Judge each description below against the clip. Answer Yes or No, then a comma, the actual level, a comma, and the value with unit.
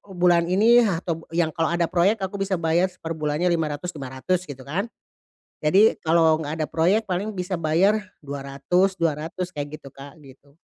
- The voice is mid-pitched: Yes, medium, 170 Hz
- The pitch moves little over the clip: No, average, 3.3 semitones